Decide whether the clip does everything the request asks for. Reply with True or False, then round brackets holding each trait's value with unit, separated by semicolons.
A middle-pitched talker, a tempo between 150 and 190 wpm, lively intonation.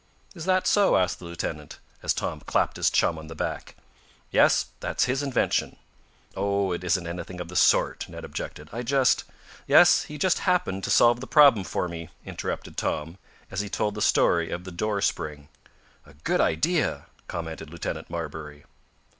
False (90 Hz; 180 wpm; 6.8 semitones)